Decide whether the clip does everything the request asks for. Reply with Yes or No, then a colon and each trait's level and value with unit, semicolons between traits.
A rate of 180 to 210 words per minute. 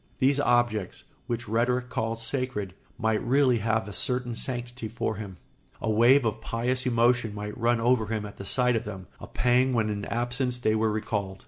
Yes: average, 190 wpm